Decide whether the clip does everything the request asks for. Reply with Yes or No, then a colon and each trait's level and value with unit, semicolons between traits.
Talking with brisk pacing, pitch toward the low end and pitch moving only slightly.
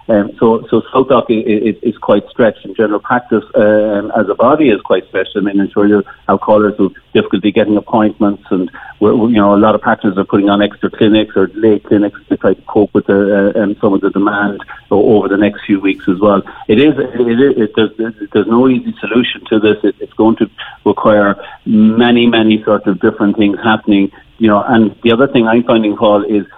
Yes: fast, 230 wpm; low, 105 Hz; narrow, 1.7 semitones